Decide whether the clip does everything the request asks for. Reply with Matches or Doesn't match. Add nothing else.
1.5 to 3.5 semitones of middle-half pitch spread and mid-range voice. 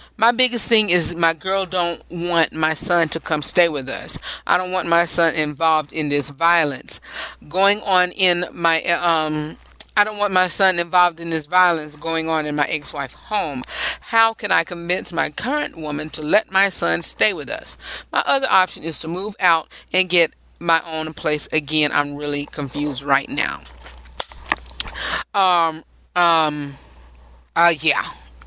Matches